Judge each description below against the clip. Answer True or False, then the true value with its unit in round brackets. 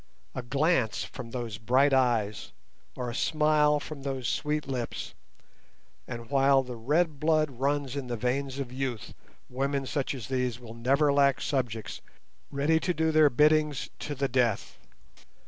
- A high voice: False (135 Hz)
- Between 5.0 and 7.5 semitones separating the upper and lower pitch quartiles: False (3.1 semitones)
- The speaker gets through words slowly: False (155 wpm)